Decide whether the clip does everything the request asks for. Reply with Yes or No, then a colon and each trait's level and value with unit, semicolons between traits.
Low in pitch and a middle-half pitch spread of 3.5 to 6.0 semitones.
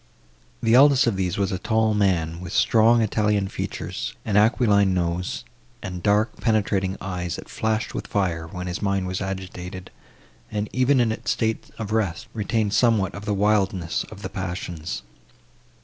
No: low, 100 Hz; average, 3.0 semitones